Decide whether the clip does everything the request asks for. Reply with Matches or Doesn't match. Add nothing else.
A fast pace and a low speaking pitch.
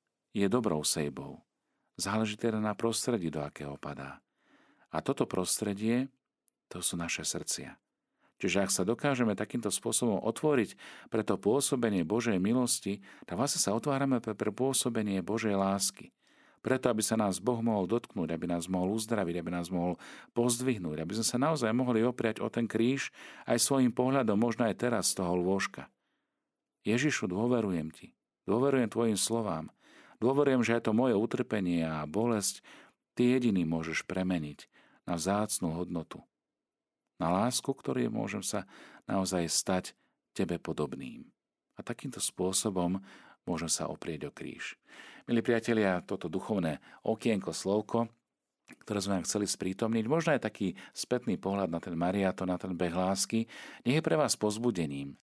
Doesn't match